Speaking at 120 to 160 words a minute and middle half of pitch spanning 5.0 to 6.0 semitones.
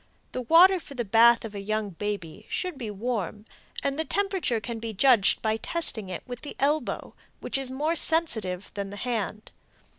No: average, 185 wpm; wide, 5.5 semitones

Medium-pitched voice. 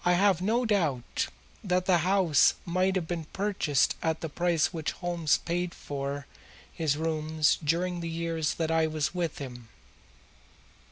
Yes: medium, 165 Hz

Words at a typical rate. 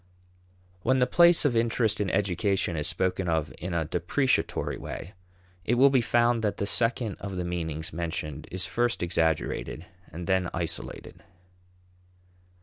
Yes: average, 145 wpm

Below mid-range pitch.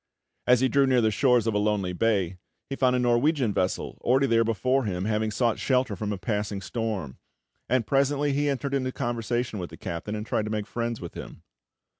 Yes: low, 115 Hz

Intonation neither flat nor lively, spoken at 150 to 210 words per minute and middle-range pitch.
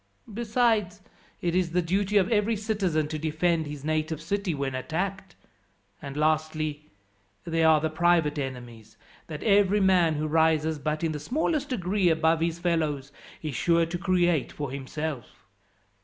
Yes: average, 3.6 semitones; average, 155 wpm; medium, 165 Hz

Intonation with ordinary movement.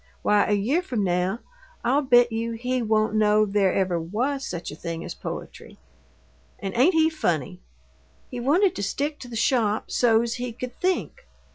Yes: average, 4.3 semitones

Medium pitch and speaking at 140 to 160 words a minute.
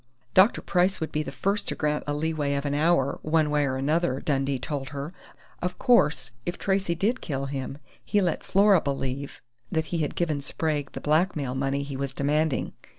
No: medium, 150 Hz; average, 195 wpm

